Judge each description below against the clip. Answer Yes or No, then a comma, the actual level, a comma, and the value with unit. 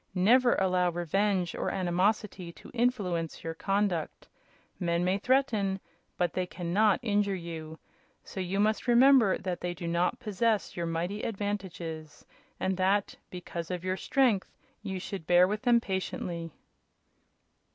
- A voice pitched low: No, high, 190 Hz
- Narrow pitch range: No, average, 3.2 semitones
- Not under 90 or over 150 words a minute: Yes, average, 140 wpm